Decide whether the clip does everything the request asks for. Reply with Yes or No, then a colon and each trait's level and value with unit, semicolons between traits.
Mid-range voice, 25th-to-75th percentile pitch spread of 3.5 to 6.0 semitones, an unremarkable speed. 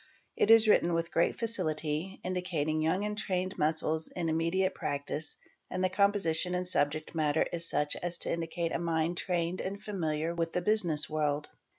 No: medium, 170 Hz; average, 2.8 semitones; average, 180 wpm